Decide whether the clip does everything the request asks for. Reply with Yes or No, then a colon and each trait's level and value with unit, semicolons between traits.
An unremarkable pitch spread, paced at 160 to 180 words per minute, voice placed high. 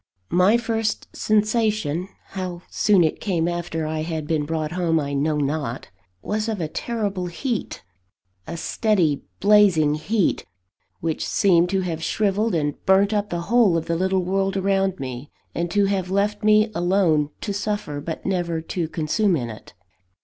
No: average, 4.3 semitones; average, 165 wpm; medium, 180 Hz